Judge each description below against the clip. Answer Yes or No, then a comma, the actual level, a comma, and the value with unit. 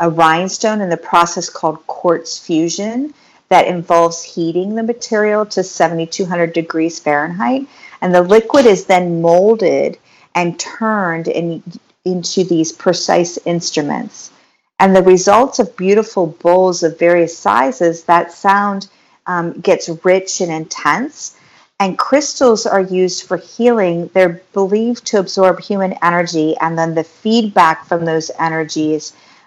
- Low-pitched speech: No, medium, 180 Hz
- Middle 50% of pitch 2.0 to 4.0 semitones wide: Yes, average, 3.3 semitones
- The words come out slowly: Yes, slow, 130 wpm